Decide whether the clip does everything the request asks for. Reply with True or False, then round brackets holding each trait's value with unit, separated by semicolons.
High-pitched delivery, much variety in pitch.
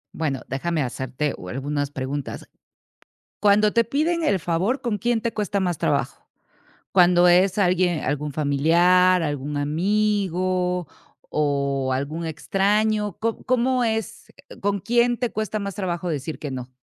False (180 Hz; 6.2 semitones)